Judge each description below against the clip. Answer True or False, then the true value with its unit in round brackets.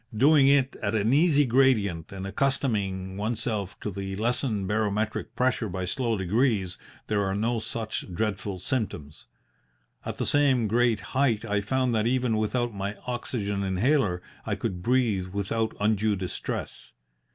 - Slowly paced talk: False (145 wpm)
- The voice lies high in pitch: False (110 Hz)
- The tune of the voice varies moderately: True (4.0 semitones)